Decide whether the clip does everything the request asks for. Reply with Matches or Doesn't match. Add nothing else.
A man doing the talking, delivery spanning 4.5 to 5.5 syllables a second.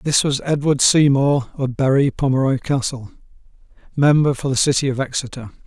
Matches